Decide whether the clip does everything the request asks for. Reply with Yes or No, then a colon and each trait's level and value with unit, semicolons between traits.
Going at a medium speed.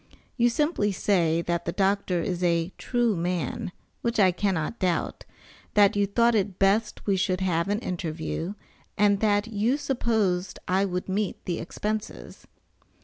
Yes: average, 150 wpm